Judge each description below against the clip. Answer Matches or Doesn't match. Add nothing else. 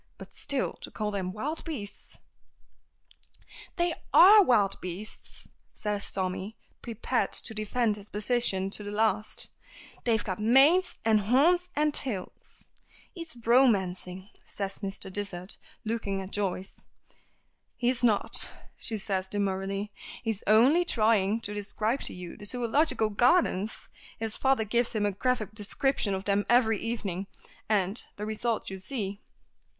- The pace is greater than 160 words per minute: Doesn't match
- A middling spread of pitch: Matches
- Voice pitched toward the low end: Doesn't match